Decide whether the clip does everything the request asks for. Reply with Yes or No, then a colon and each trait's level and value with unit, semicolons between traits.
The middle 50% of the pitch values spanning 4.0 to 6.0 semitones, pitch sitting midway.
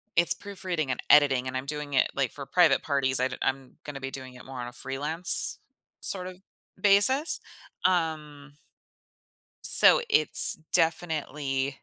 Yes: average, 4.3 semitones; medium, 145 Hz